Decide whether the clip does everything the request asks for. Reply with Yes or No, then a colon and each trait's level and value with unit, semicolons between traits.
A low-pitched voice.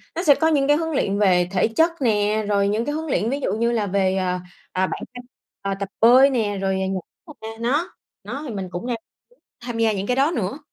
No: high, 220 Hz